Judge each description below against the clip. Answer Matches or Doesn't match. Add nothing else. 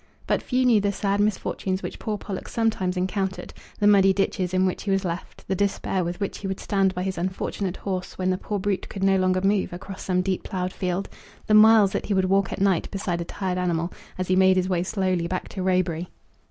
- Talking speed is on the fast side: Matches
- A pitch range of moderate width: Doesn't match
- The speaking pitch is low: Doesn't match